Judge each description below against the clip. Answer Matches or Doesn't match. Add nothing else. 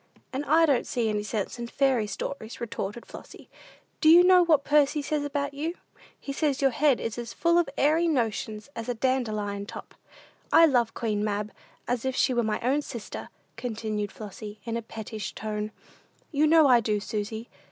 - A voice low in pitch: Doesn't match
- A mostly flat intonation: Doesn't match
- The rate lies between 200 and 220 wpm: Doesn't match